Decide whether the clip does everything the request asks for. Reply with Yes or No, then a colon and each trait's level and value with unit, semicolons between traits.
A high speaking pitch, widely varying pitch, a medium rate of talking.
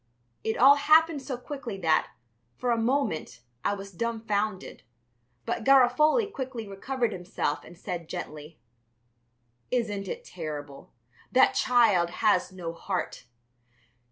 No: high, 215 Hz; wide, 6.3 semitones; slow, 120 wpm